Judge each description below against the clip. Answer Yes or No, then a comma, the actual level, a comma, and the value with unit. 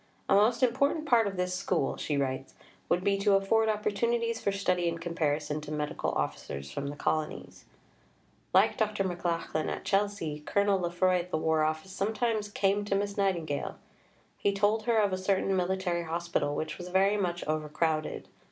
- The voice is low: No, medium, 185 Hz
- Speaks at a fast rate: No, average, 170 wpm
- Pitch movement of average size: Yes, average, 4.4 semitones